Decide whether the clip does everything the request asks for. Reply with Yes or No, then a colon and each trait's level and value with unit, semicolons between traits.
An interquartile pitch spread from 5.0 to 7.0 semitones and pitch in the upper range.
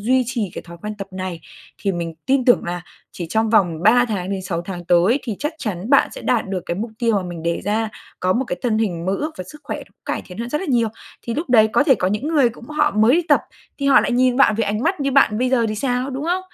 Yes: wide, 5.6 semitones; high, 220 Hz